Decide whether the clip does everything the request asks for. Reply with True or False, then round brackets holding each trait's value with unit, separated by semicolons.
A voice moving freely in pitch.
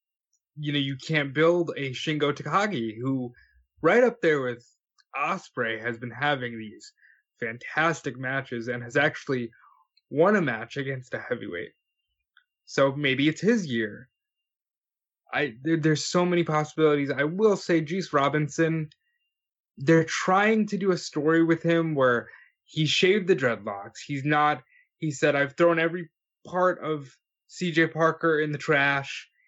False (3.7 semitones)